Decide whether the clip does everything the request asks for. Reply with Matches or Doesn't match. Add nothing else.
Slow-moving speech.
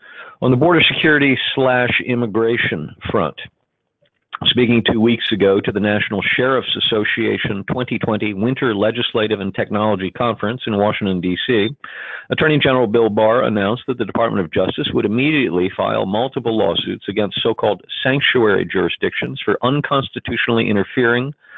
Matches